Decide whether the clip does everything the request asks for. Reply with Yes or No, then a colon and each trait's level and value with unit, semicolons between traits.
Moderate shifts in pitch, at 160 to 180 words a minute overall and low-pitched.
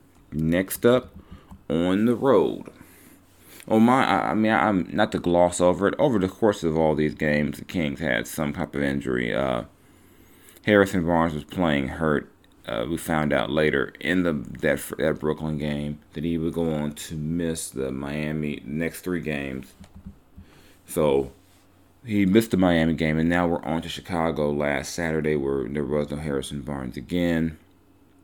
Yes: average, 3.6 semitones; average, 170 wpm; very low, 80 Hz